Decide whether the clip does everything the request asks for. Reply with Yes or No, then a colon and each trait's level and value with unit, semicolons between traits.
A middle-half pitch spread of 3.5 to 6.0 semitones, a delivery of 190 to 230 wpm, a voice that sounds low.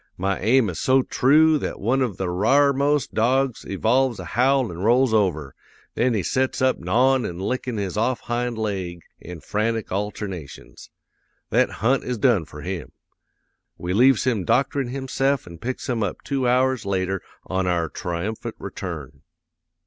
No: wide, 5.6 semitones; average, 160 wpm; low, 115 Hz